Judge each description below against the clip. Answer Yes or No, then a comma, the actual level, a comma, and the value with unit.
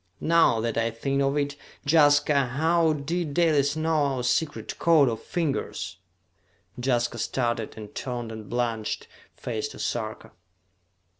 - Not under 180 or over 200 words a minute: No, slow, 135 wpm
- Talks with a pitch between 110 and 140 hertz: Yes, low, 135 Hz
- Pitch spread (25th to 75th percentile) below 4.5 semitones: Yes, average, 4.1 semitones